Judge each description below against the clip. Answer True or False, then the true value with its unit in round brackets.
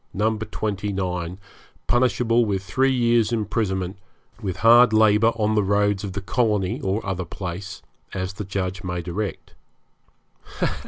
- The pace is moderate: False (125 wpm)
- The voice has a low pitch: True (100 Hz)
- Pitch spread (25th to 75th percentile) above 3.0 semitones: False (2.7 semitones)